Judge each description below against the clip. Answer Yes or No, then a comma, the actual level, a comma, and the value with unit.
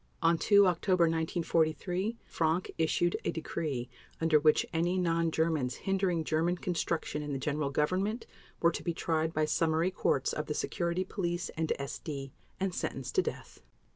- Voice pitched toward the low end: No, medium, 165 Hz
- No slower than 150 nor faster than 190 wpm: Yes, average, 160 wpm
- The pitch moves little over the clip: Yes, narrow, 2.3 semitones